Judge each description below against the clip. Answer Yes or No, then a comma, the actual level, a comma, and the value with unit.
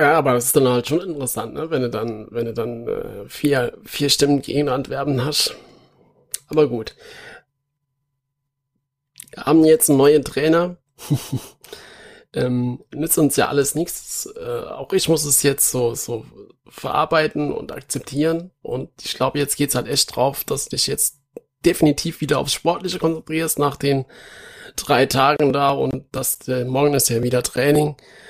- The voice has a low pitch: No, medium, 145 Hz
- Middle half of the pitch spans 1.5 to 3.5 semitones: Yes, average, 2.8 semitones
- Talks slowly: No, average, 165 wpm